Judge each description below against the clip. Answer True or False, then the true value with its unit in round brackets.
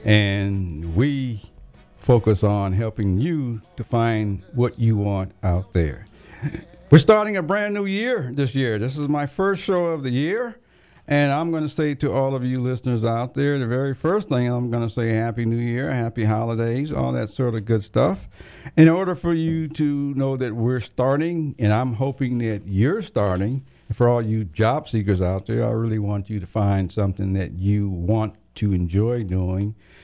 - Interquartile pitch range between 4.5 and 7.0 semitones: True (5.2 semitones)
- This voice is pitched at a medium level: False (120 Hz)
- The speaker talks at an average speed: True (190 wpm)